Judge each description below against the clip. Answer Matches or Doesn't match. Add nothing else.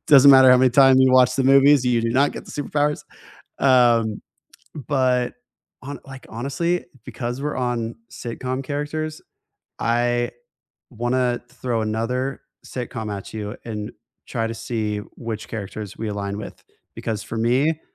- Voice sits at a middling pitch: Doesn't match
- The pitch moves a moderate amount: Matches